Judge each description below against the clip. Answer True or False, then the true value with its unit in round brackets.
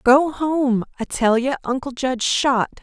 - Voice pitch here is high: True (260 Hz)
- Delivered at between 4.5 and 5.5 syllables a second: False (3.8 syllables/s)